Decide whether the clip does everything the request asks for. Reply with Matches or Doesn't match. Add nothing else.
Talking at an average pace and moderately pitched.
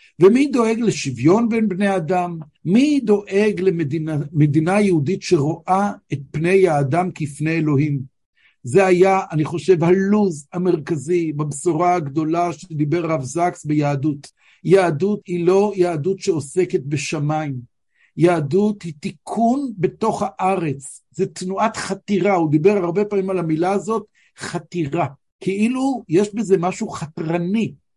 Matches